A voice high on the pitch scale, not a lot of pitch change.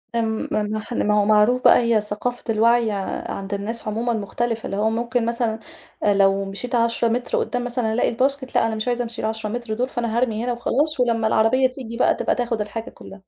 Yes: high, 230 Hz; narrow, 2.0 semitones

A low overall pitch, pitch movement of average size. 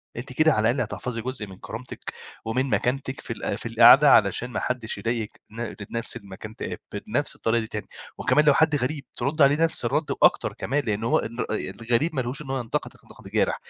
Yes: low, 125 Hz; average, 3.4 semitones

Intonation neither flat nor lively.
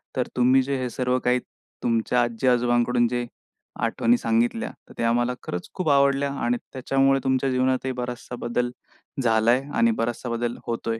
No: narrow, 2.1 semitones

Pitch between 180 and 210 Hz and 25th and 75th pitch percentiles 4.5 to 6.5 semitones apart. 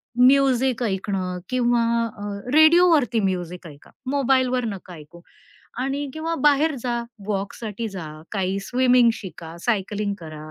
No: high, 230 Hz; wide, 5.4 semitones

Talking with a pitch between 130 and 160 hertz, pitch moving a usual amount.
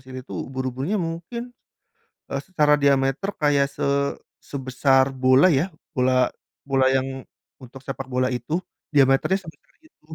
No: low, 135 Hz; narrow, 2.2 semitones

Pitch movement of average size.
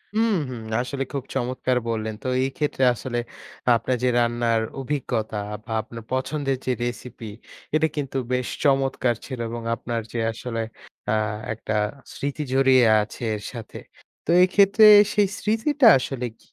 Yes: average, 3.2 semitones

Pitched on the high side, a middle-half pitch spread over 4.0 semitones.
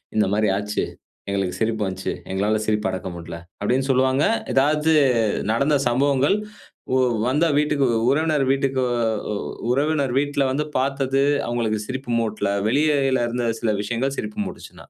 No: low, 130 Hz; average, 4.5 semitones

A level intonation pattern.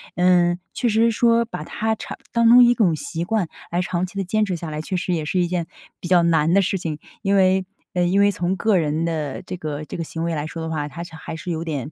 No: average, 3.4 semitones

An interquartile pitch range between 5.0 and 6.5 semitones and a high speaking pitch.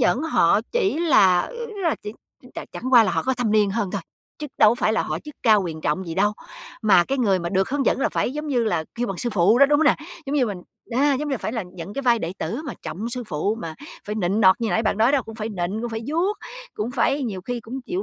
Yes: wide, 5.5 semitones; high, 225 Hz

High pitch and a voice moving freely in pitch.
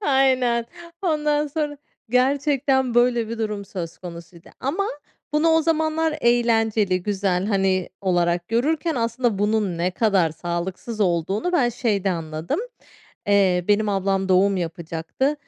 Yes: high, 215 Hz; wide, 6.3 semitones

